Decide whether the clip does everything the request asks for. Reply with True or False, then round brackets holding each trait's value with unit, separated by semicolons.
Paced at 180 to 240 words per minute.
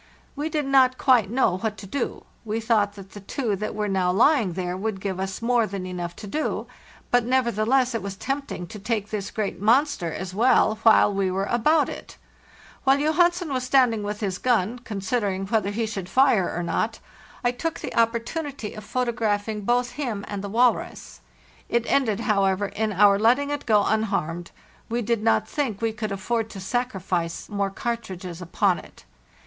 True (185 wpm)